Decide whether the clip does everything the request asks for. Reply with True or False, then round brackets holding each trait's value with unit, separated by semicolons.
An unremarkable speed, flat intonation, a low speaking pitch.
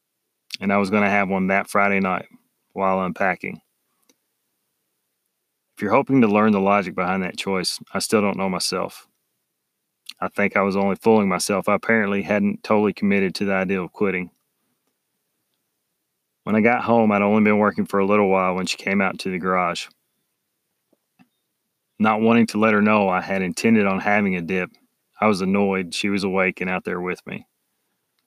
True (185 wpm; 1.7 semitones; 100 Hz)